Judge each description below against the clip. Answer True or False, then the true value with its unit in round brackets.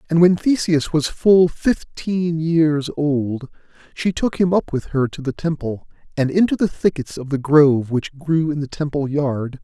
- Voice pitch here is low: False (155 Hz)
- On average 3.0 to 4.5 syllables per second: True (4.3 syllables/s)